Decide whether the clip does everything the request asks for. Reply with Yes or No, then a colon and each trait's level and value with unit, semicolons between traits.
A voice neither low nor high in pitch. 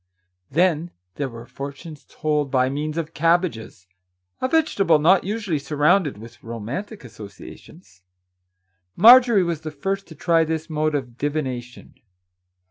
Yes: medium, 150 Hz